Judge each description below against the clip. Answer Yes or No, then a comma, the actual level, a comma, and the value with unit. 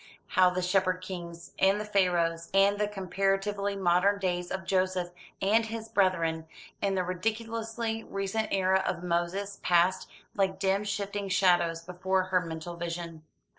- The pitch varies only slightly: Yes, narrow, 2.2 semitones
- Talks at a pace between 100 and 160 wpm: Yes, average, 145 wpm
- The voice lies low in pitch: No, high, 190 Hz